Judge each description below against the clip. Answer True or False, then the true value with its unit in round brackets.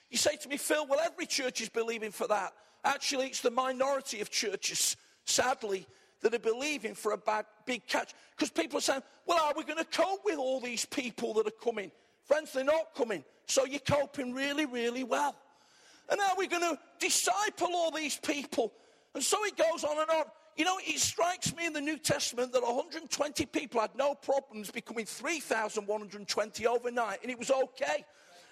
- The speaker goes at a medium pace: True (195 wpm)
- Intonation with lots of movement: False (4.9 semitones)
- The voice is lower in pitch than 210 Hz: False (280 Hz)